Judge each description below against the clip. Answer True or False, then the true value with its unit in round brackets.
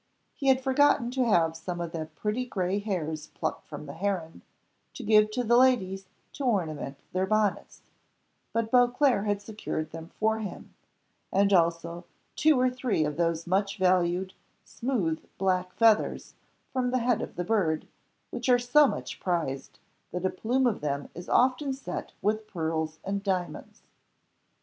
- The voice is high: True (195 Hz)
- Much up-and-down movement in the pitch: True (6.1 semitones)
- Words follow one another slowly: False (160 wpm)